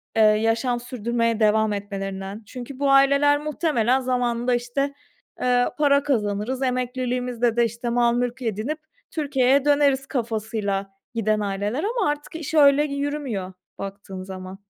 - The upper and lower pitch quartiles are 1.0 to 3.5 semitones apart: No, average, 4.3 semitones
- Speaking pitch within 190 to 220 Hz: No, high, 245 Hz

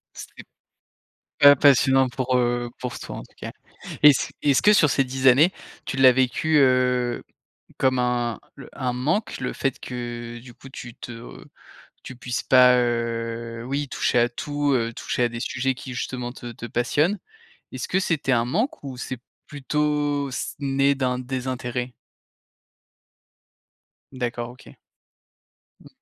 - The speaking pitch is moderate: No, low, 125 Hz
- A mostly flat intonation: Yes, narrow, 2.1 semitones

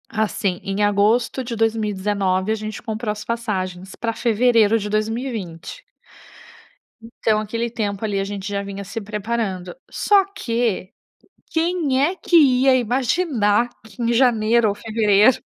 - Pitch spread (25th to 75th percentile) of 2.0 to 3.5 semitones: Yes, average, 2.7 semitones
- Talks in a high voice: Yes, high, 220 Hz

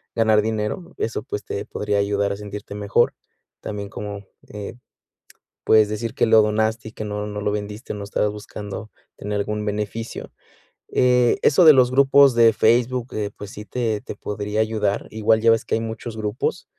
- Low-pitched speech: Yes, low, 105 Hz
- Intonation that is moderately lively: No, narrow, 1.7 semitones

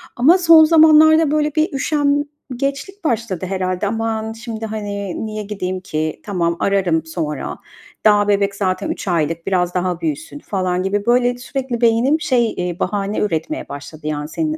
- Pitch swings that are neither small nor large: No, wide, 7.1 semitones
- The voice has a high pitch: Yes, high, 210 Hz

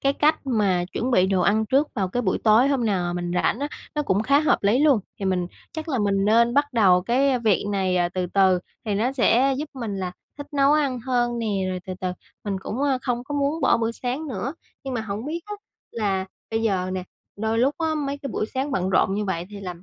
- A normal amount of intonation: No, wide, 6.1 semitones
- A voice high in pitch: Yes, high, 230 Hz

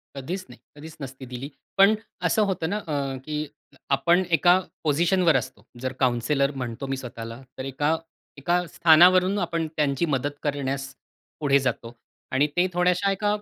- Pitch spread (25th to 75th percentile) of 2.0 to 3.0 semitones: No, average, 4.8 semitones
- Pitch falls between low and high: Yes, medium, 145 Hz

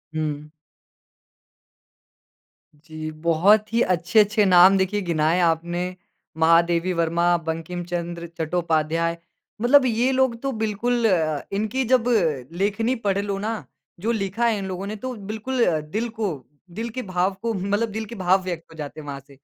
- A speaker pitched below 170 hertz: No, medium, 185 Hz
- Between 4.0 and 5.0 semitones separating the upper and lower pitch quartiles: Yes, average, 4.7 semitones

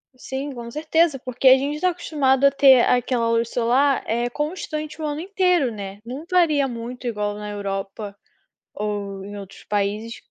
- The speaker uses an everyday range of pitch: No, wide, 5.8 semitones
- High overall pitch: Yes, very high, 250 Hz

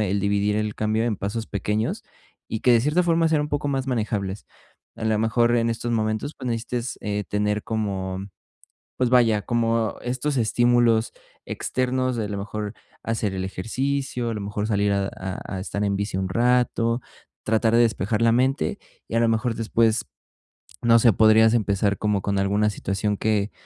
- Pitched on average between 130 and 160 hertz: No, low, 110 Hz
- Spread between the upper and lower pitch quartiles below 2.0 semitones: No, narrow, 2.6 semitones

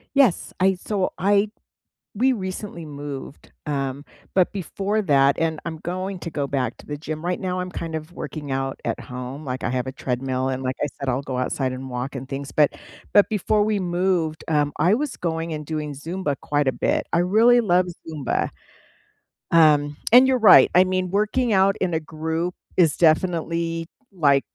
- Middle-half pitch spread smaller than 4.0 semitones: No, average, 4.8 semitones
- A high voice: No, medium, 160 Hz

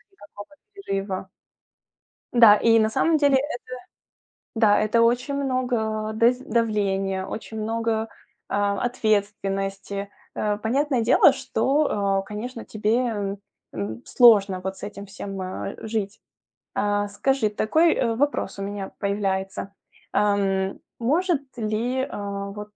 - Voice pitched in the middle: No, high, 215 Hz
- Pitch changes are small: No, average, 3.3 semitones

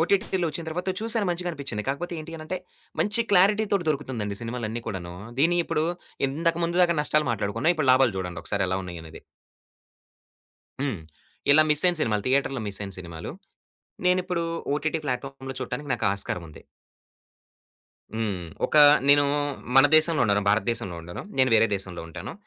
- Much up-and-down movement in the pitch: Yes, wide, 8.3 semitones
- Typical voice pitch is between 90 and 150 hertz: Yes, low, 135 Hz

